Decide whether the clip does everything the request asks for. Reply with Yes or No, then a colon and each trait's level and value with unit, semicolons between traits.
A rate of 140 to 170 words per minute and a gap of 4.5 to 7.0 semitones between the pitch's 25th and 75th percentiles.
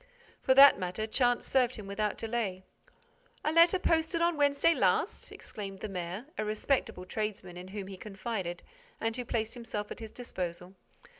Yes: average, 165 wpm; average, 4.8 semitones